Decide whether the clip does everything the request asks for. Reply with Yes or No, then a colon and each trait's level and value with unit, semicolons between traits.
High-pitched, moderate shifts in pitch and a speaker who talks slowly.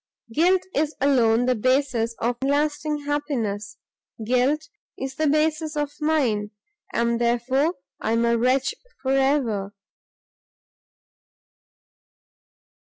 Yes: very high, 265 Hz; average, 4.0 semitones; slow, 105 wpm